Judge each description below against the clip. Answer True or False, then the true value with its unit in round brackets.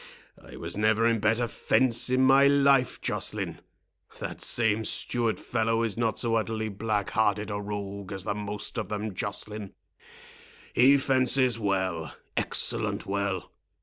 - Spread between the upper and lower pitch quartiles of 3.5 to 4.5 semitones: False (2.8 semitones)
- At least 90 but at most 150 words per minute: True (140 wpm)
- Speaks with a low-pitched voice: True (110 Hz)